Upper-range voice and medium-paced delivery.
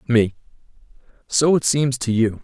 No: low, 125 Hz; average, 150 wpm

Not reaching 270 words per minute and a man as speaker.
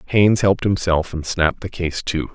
Yes: fast, 205 wpm; male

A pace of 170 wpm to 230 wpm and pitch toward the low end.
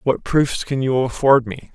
Yes: fast, 205 wpm; low, 130 Hz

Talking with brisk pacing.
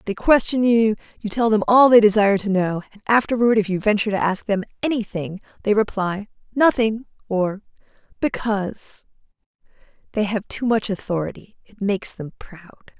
No: average, 155 wpm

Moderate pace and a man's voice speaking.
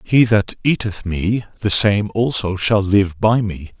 Yes: average, 175 wpm; male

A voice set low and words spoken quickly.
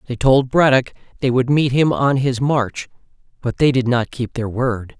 Yes: low, 125 Hz; fast, 215 wpm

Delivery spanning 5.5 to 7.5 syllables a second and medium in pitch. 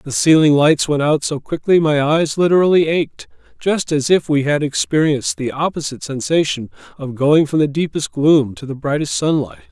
No: 5.1 syllables/s; medium, 150 Hz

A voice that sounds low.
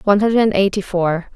No: high, 195 Hz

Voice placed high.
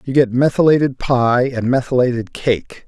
No: low, 125 Hz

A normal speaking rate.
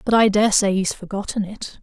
No: fast, 230 wpm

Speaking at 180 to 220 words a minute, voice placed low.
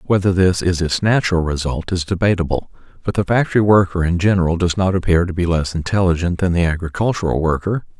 Yes: average, 190 wpm; very low, 90 Hz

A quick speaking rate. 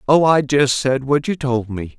Yes: fast, 240 wpm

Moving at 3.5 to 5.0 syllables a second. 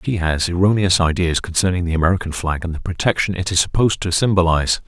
No: 6.7 syllables/s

